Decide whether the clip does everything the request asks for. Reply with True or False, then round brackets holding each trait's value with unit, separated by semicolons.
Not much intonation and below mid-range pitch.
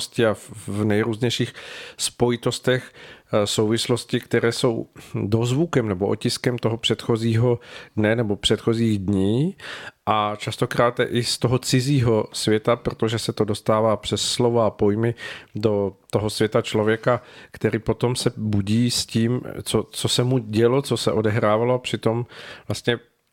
True (2.2 semitones; 115 Hz)